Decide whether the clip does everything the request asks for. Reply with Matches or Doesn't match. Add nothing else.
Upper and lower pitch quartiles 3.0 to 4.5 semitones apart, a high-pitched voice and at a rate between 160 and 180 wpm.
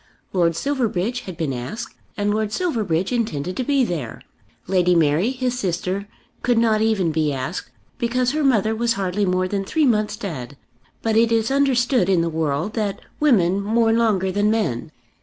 Doesn't match